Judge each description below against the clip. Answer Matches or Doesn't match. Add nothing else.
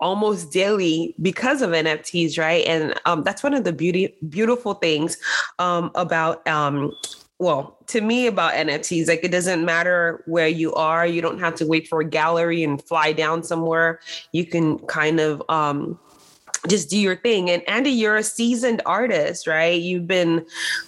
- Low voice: Doesn't match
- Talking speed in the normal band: Matches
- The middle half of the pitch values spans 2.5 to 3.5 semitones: Matches